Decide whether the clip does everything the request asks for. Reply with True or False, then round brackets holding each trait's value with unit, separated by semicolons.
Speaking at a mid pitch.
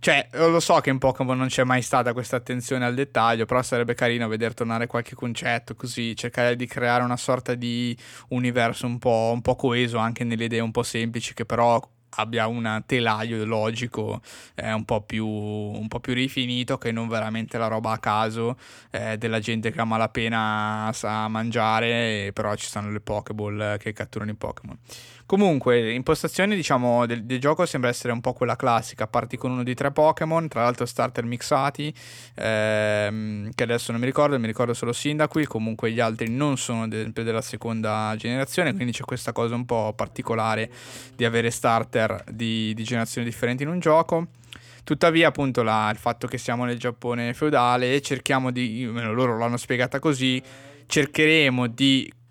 False (120 Hz)